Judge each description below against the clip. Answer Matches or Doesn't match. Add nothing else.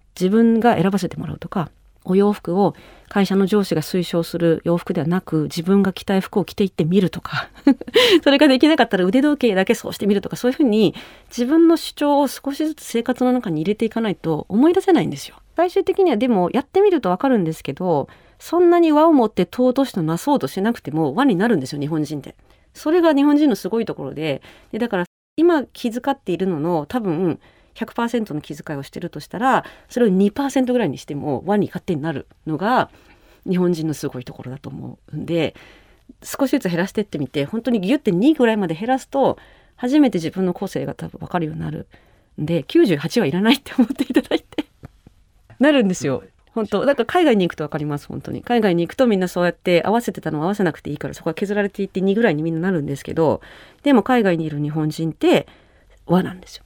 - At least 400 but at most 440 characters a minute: Matches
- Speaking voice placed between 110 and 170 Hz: Doesn't match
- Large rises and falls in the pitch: Matches